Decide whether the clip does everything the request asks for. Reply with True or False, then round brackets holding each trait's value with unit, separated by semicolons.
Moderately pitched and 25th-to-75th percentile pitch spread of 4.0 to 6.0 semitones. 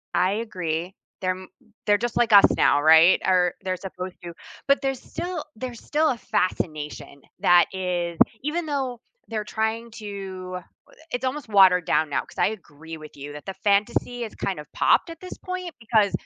False (195 Hz; 5.2 semitones)